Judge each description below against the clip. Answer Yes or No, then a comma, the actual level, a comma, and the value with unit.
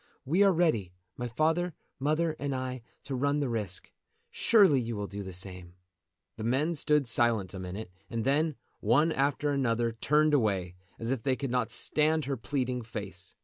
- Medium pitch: No, low, 125 Hz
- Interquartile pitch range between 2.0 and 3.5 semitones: No, average, 5.2 semitones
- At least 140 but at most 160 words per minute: No, average, 180 wpm